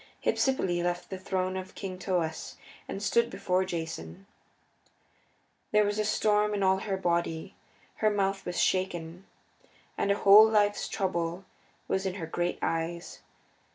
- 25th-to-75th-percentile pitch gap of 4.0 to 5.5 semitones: No, average, 2.7 semitones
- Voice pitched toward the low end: No, high, 190 Hz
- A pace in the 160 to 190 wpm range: No, average, 145 wpm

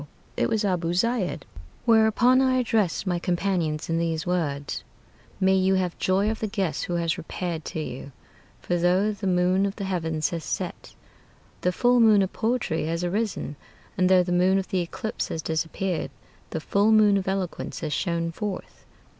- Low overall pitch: No, medium, 185 Hz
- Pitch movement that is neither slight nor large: Yes, average, 3.4 semitones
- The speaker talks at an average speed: Yes, average, 180 wpm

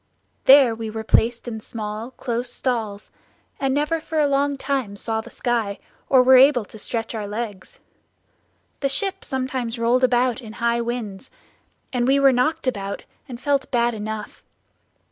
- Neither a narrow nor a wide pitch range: Yes, average, 3.2 semitones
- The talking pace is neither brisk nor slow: Yes, average, 165 wpm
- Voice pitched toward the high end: Yes, high, 240 Hz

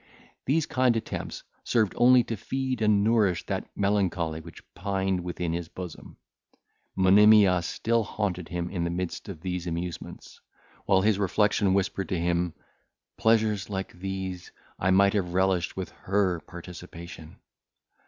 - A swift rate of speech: No, average, 140 wpm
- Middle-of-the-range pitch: No, very low, 95 Hz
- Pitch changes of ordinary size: Yes, average, 3.0 semitones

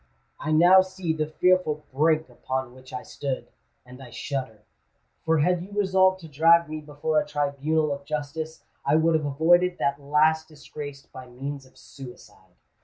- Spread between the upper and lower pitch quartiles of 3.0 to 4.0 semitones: No, narrow, 2.6 semitones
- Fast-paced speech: No, average, 165 wpm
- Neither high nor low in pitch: Yes, medium, 150 Hz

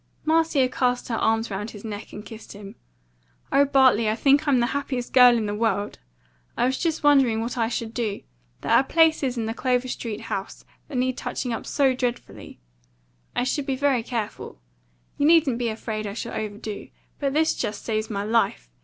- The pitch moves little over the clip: No, average, 3.6 semitones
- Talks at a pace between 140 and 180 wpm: No, average, 195 wpm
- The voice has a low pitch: No, high, 240 Hz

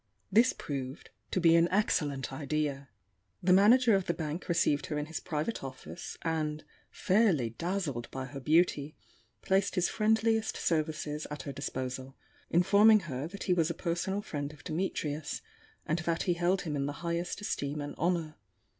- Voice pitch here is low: No, medium, 160 Hz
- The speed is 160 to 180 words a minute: Yes, average, 165 wpm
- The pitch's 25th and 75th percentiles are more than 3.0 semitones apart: Yes, average, 4.0 semitones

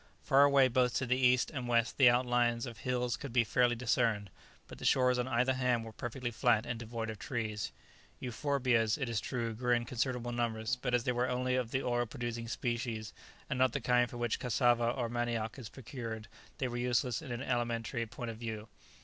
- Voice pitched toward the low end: Yes, low, 120 Hz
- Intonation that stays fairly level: Yes, narrow, 1.5 semitones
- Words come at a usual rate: No, fast, 210 wpm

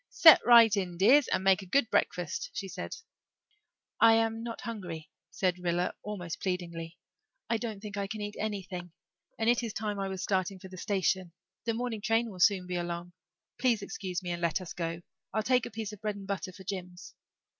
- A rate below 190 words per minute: No, fast, 205 wpm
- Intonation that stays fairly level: No, average, 3.7 semitones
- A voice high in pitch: Yes, high, 195 Hz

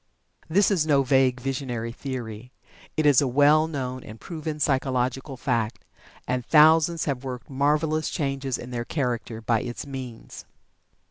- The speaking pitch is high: No, low, 135 Hz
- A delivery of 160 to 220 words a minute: No, average, 145 wpm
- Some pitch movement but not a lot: Yes, average, 3.3 semitones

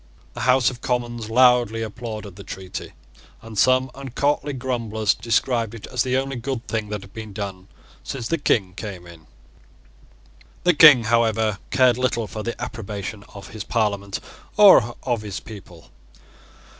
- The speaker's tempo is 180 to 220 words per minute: No, average, 155 wpm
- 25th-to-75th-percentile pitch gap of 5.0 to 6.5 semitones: No, average, 3.5 semitones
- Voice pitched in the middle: No, low, 115 Hz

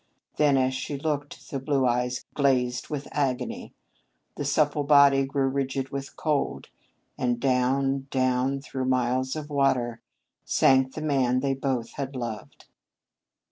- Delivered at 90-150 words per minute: Yes, average, 140 wpm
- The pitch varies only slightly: Yes, narrow, 1.7 semitones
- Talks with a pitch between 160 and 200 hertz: No, low, 135 Hz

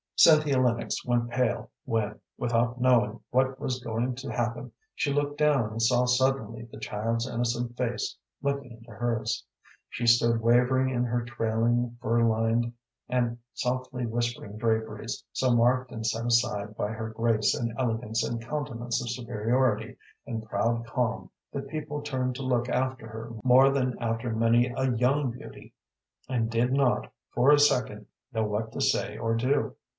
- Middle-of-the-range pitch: No, low, 120 Hz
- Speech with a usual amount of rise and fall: No, narrow, 2.0 semitones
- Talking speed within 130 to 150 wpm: No, average, 160 wpm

